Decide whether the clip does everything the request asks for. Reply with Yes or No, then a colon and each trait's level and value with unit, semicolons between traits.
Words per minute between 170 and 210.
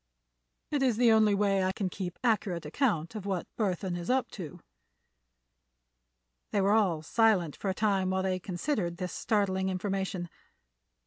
No: average, 155 wpm